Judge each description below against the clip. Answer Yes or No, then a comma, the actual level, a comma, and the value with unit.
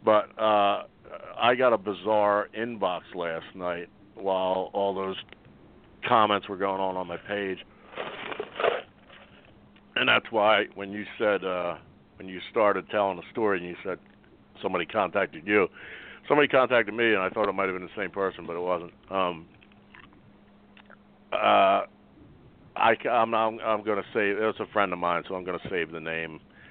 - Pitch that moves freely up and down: No, narrow, 2.6 semitones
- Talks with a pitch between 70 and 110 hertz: Yes, very low, 95 Hz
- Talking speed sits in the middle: Yes, average, 170 wpm